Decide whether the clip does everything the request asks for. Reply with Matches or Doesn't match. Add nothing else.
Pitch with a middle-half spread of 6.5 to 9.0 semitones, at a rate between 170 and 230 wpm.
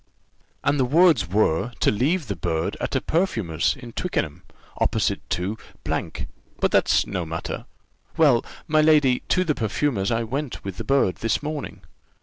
Doesn't match